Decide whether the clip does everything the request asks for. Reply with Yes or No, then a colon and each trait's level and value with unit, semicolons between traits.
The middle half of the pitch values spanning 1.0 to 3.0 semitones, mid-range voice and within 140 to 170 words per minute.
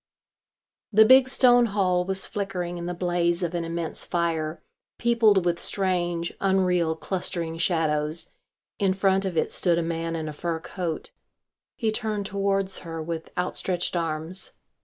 Yes: average, 2.7 semitones; medium, 175 Hz; average, 150 wpm